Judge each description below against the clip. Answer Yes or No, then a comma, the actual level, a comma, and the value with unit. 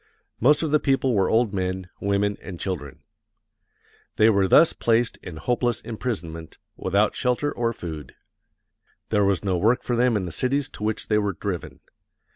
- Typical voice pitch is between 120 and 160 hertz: No, low, 105 Hz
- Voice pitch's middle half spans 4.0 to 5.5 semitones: Yes, average, 4.5 semitones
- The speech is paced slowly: No, average, 170 wpm